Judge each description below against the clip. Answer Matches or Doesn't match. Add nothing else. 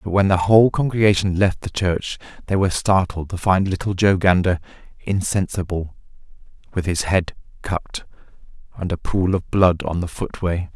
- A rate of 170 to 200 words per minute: Doesn't match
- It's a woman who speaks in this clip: Doesn't match